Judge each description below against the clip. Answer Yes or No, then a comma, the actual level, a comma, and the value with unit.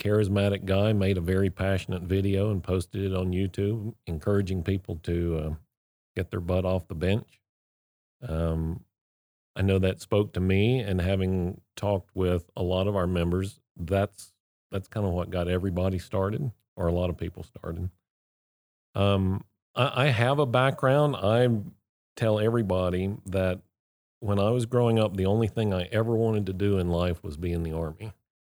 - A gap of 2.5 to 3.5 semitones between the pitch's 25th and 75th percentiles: Yes, average, 2.8 semitones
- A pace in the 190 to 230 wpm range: No, average, 175 wpm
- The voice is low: Yes, very low, 95 Hz